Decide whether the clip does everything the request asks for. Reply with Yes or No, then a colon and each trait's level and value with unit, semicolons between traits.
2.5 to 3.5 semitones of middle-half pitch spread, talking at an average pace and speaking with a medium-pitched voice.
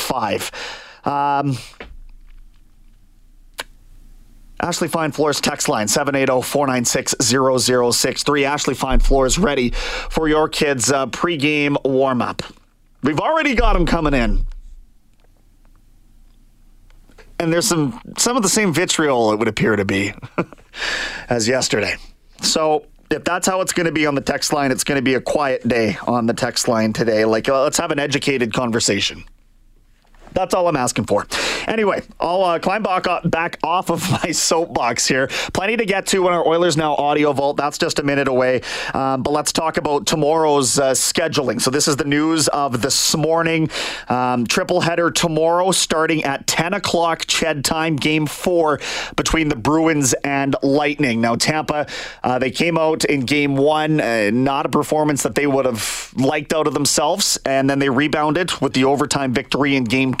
No: average, 4.0 semitones; average, 165 wpm; medium, 145 Hz